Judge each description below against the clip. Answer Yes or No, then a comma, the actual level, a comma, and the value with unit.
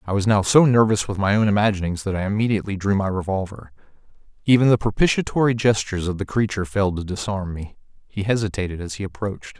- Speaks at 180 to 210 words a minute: Yes, average, 195 wpm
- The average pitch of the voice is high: No, low, 100 Hz